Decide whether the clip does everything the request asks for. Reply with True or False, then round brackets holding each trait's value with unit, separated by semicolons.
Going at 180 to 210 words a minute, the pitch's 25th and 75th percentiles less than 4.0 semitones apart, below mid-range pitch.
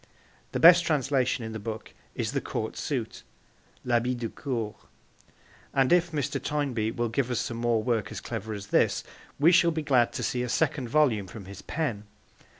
False (185 wpm; 4.5 semitones; 120 Hz)